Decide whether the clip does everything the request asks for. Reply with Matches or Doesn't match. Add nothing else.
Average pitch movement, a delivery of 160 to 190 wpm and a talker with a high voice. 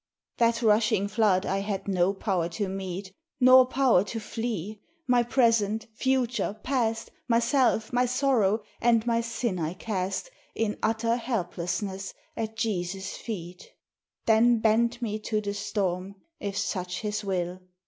Doesn't match